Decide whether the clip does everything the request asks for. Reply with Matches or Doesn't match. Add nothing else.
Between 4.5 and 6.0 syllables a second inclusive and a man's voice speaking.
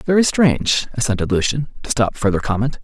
Matches